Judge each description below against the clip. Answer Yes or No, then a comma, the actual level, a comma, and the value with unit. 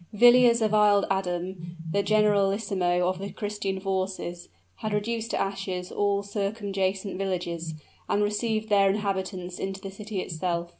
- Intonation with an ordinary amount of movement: No, narrow, 1.9 semitones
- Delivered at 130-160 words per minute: Yes, average, 140 wpm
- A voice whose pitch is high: Yes, high, 195 Hz